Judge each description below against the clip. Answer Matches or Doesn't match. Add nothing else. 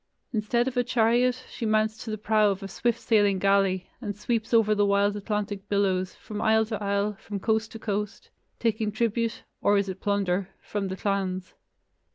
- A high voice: Matches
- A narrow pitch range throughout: Matches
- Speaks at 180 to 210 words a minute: Matches